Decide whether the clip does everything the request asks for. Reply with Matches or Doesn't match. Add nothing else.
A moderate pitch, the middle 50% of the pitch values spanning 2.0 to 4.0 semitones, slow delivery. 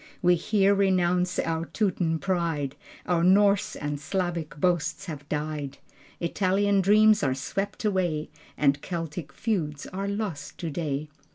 Doesn't match